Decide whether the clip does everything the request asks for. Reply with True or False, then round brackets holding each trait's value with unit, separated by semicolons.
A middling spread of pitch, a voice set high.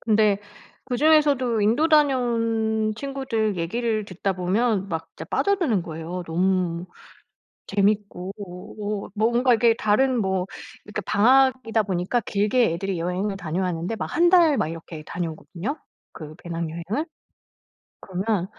True (5.0 semitones; 210 Hz)